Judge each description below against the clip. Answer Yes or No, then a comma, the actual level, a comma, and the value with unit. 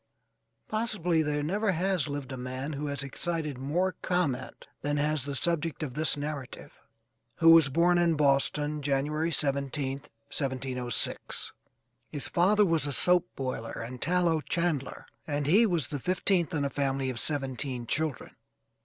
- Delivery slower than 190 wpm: Yes, average, 150 wpm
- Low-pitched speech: No, medium, 150 Hz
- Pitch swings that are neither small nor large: Yes, average, 3.6 semitones